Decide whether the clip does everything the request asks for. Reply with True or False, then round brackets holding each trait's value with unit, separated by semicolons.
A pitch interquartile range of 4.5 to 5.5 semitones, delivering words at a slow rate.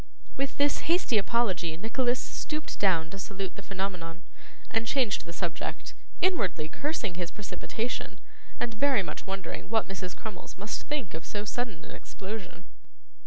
False (4.8 semitones; 150 wpm)